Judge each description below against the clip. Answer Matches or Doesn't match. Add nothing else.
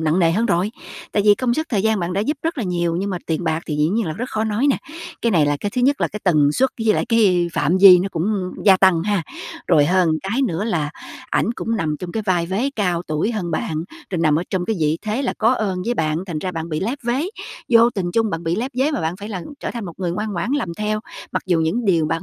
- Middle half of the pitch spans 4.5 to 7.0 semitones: Matches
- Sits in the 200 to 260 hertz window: Doesn't match